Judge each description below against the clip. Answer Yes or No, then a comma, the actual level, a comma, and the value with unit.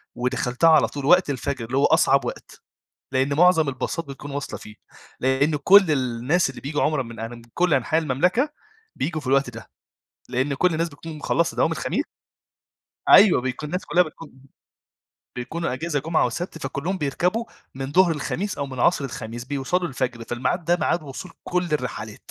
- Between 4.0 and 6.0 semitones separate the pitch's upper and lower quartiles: Yes, average, 4.5 semitones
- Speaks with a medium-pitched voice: Yes, medium, 145 Hz